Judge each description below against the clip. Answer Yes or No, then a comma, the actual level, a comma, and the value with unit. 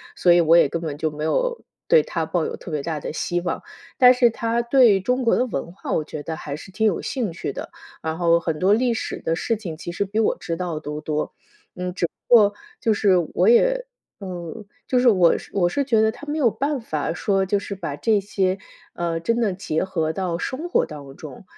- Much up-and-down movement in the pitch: Yes, wide, 5.8 semitones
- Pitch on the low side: No, high, 190 Hz